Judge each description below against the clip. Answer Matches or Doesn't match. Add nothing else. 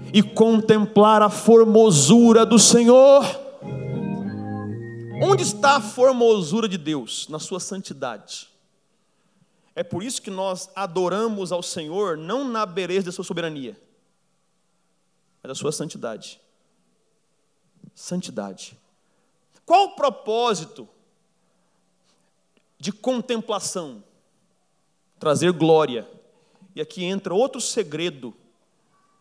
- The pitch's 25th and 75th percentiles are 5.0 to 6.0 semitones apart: Matches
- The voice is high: Matches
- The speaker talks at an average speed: Doesn't match